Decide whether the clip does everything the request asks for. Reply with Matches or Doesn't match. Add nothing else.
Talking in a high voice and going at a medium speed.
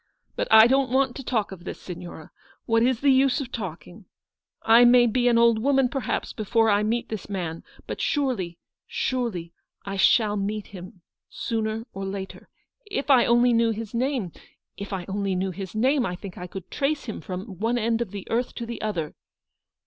Matches